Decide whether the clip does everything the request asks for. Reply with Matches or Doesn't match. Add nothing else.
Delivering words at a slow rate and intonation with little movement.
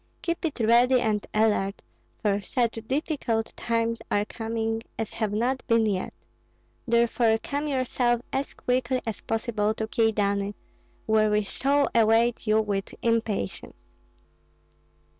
Matches